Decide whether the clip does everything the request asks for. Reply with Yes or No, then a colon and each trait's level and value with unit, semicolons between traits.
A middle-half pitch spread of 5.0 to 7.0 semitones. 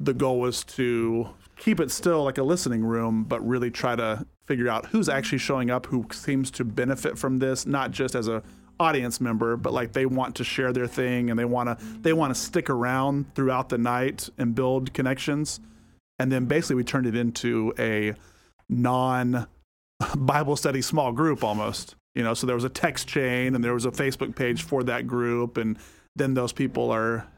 No: narrow, 2.5 semitones